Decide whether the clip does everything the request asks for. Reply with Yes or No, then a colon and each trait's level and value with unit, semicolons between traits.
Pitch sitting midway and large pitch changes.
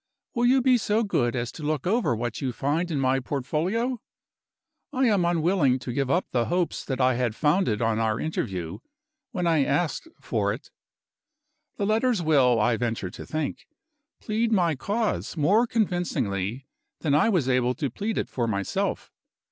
Yes: medium, 150 Hz; wide, 8.3 semitones